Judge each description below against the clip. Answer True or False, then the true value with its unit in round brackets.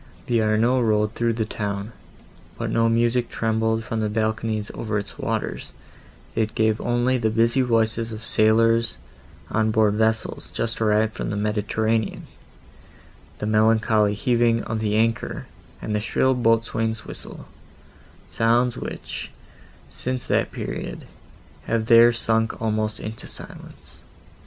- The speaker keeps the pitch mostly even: True (1.1 semitones)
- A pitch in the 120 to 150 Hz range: False (110 Hz)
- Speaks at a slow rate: True (130 wpm)